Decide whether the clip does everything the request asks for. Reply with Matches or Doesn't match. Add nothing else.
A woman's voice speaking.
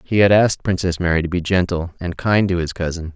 Doesn't match